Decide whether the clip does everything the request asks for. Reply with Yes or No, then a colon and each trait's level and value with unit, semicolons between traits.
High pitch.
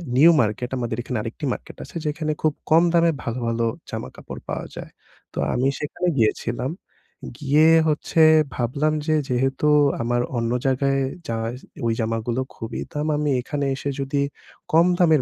No: low, 135 Hz